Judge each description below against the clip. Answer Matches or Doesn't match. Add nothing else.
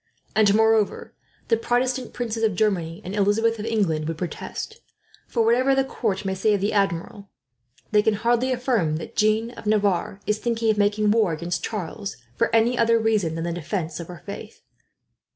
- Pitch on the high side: Matches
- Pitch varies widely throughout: Doesn't match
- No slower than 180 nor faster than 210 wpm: Matches